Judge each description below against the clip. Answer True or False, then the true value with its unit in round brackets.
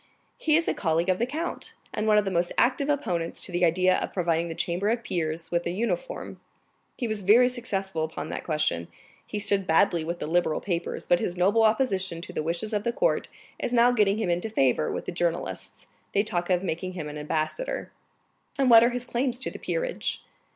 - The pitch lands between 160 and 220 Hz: True (190 Hz)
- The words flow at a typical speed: False (220 wpm)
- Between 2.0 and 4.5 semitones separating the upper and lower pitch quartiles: False (5.5 semitones)